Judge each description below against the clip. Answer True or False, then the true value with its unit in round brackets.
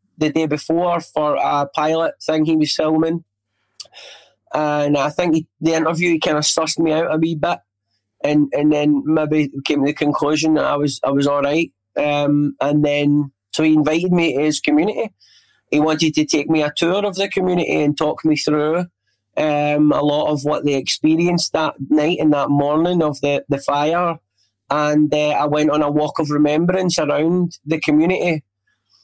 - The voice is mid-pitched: True (150 Hz)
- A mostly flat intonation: True (1.7 semitones)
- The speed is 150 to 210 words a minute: True (190 wpm)